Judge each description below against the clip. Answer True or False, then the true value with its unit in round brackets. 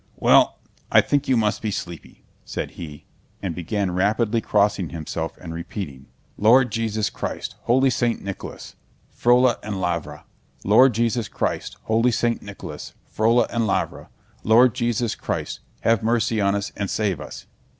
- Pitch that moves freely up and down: False (3.5 semitones)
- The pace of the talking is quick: False (150 wpm)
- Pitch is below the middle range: True (110 Hz)